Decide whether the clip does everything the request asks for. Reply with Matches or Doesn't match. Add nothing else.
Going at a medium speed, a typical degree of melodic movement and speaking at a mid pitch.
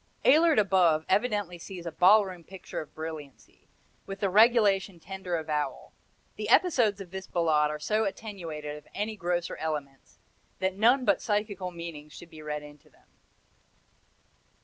Matches